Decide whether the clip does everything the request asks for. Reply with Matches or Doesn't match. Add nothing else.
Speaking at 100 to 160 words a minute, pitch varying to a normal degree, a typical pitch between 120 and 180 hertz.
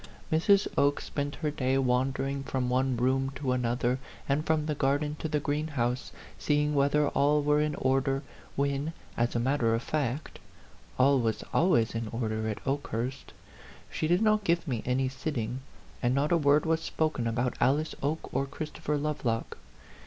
Doesn't match